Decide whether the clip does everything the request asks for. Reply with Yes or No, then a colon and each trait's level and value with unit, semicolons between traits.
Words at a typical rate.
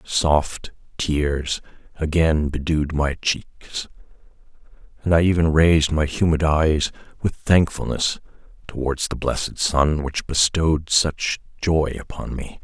No: slow, 120 wpm